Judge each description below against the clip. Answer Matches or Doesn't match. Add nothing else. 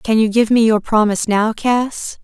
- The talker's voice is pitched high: Matches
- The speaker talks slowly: Doesn't match